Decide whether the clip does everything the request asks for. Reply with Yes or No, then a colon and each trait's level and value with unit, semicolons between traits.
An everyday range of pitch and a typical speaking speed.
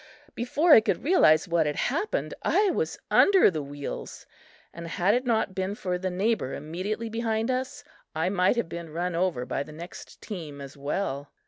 No: wide, 6.5 semitones; average, 185 wpm